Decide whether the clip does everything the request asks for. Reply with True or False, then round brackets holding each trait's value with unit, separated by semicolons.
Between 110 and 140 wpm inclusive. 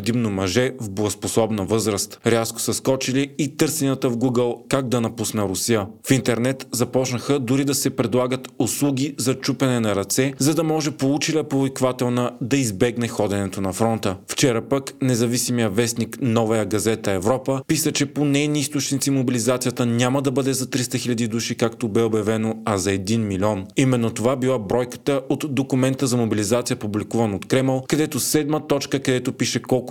False (165 wpm)